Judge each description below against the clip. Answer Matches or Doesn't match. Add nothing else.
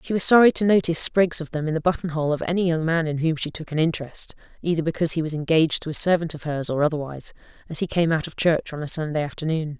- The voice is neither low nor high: Matches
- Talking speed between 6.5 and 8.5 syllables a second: Matches